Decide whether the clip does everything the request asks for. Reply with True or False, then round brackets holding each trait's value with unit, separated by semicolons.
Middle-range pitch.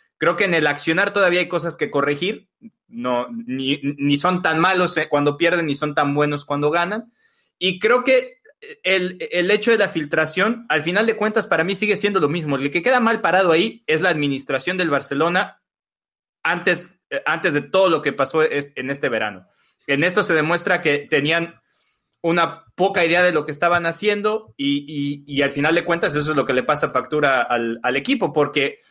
True (165 Hz)